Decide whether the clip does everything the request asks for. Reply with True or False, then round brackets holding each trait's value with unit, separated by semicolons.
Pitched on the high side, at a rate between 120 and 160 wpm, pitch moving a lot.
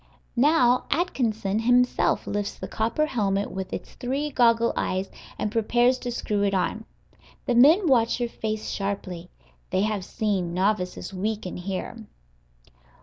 False (220 Hz; 140 wpm; 3.8 semitones)